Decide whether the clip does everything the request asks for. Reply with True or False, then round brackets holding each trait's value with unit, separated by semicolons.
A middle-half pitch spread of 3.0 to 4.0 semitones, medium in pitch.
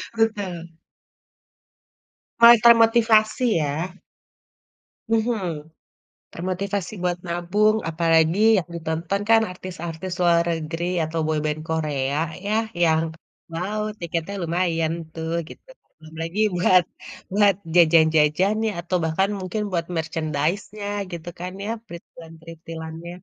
True (3.7 semitones; 170 Hz)